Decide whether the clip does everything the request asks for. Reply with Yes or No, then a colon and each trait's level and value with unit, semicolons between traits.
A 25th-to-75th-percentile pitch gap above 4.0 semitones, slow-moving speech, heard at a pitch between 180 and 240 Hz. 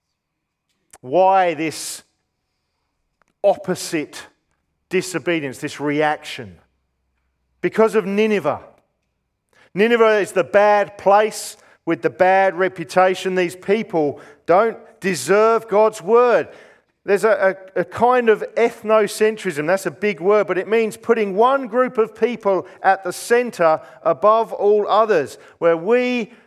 Yes: average, 4.6 semitones; slow, 115 wpm; high, 190 Hz